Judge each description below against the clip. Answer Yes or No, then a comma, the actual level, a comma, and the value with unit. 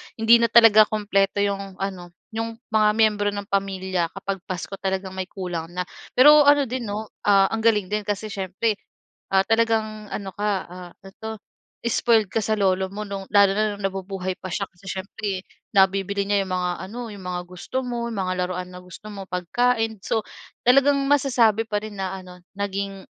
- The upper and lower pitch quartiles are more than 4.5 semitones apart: No, average, 2.7 semitones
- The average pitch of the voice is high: Yes, high, 200 Hz